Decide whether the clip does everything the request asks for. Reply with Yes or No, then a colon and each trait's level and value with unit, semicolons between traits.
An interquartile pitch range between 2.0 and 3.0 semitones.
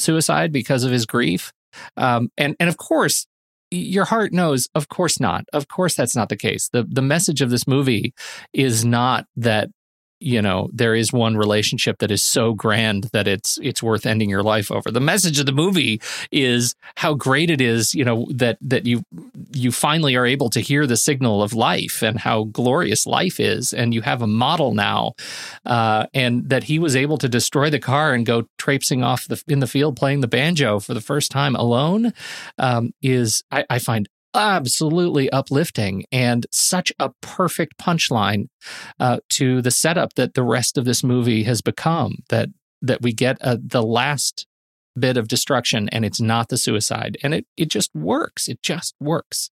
No: average, 3.9 semitones